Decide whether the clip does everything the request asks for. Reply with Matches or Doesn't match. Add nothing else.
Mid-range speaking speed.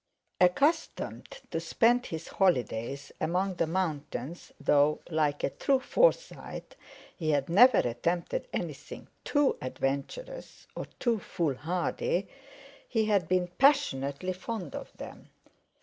Doesn't match